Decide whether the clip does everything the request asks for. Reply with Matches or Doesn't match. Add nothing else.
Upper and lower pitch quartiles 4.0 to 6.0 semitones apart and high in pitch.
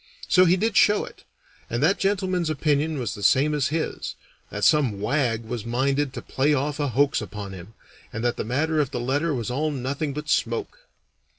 Doesn't match